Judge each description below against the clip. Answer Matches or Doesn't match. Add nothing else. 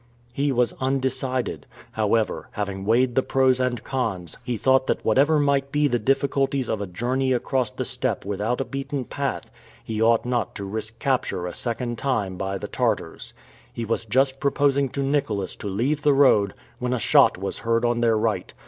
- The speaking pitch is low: Matches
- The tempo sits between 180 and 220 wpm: Matches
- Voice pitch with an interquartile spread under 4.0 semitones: Matches